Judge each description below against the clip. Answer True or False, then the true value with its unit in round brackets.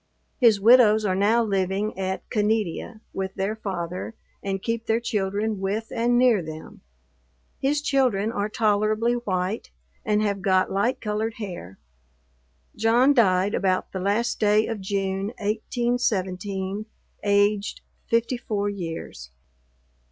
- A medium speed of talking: False (120 wpm)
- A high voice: True (210 Hz)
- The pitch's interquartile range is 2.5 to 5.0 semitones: True (2.8 semitones)